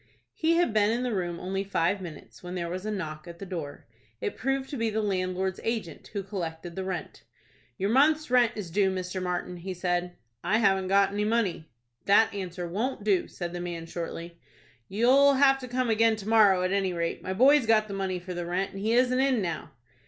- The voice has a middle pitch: No, high, 195 Hz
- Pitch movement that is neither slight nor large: Yes, average, 4.1 semitones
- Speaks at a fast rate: Yes, fast, 220 wpm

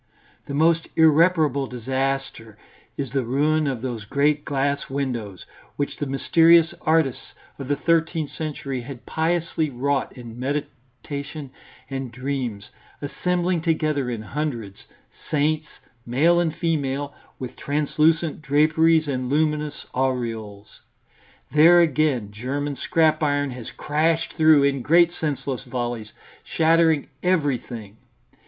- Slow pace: Yes, slow, 115 wpm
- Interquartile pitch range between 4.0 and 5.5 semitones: No, average, 3.6 semitones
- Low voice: No, medium, 145 Hz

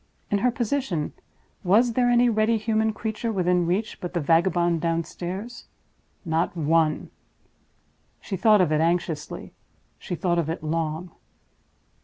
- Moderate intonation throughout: Yes, average, 4.8 semitones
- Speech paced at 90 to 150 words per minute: Yes, slow, 135 wpm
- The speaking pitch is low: No, medium, 180 Hz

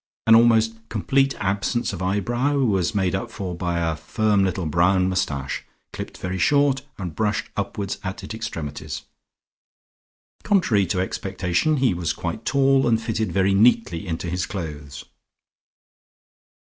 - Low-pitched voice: Yes, low, 100 Hz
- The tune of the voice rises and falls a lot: No, average, 4.2 semitones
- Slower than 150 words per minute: Yes, average, 140 wpm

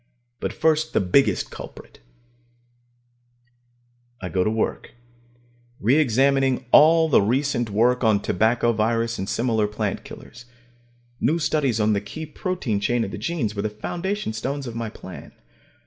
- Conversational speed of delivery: Yes, average, 150 wpm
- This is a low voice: Yes, low, 120 Hz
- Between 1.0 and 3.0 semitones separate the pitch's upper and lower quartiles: No, average, 4.8 semitones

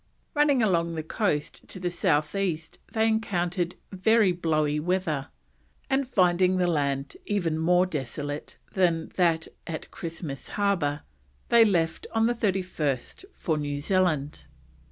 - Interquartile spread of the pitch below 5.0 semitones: Yes, average, 4.1 semitones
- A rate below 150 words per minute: Yes, slow, 135 wpm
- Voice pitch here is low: No, medium, 175 Hz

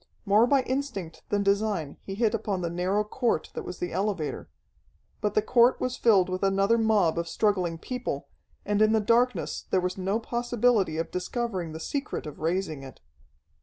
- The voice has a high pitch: Yes, high, 200 Hz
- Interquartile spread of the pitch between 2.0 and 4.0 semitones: No, average, 4.4 semitones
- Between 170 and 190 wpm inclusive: Yes, average, 180 wpm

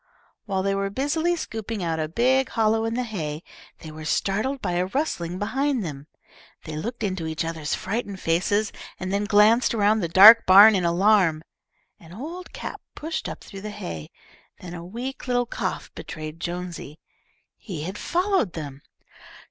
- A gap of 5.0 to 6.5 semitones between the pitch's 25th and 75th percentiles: Yes, wide, 5.5 semitones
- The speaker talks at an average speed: Yes, average, 170 wpm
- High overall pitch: Yes, high, 195 Hz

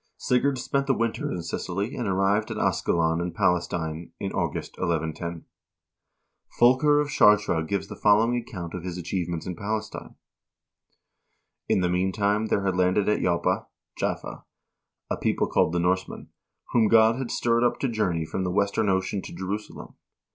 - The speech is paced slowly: No, average, 170 wpm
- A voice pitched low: Yes, very low, 95 Hz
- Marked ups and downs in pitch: No, average, 4.0 semitones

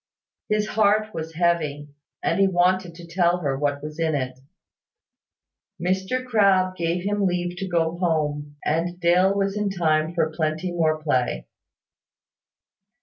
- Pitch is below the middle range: No, medium, 170 Hz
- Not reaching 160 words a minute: Yes, average, 145 wpm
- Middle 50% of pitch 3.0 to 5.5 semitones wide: Yes, average, 3.3 semitones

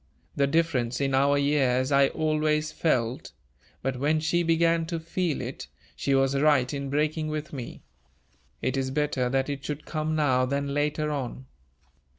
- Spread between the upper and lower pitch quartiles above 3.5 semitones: No, narrow, 2.5 semitones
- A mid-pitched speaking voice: Yes, medium, 145 Hz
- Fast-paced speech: No, average, 165 wpm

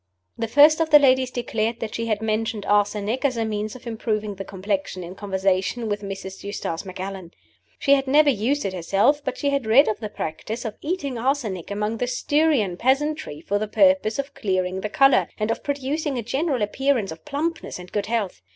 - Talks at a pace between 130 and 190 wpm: No, average, 200 wpm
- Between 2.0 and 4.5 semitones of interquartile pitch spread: No, wide, 5.4 semitones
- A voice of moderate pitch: No, high, 225 Hz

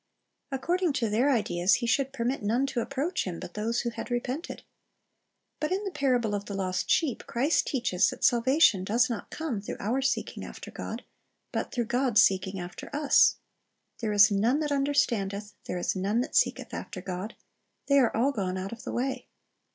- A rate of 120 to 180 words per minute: No, average, 190 wpm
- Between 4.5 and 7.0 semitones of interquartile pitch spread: Yes, average, 5.2 semitones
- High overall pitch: Yes, high, 235 Hz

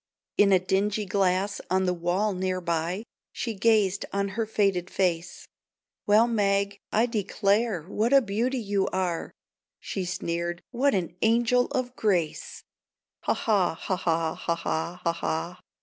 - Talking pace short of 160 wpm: Yes, average, 150 wpm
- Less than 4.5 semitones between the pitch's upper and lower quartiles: Yes, average, 3.3 semitones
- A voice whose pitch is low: No, high, 195 Hz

